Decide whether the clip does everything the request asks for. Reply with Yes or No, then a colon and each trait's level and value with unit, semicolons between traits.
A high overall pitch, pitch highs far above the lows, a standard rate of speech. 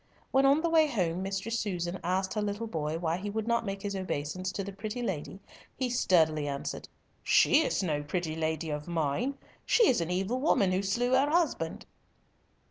Yes: high, 195 Hz; wide, 6.0 semitones; average, 195 wpm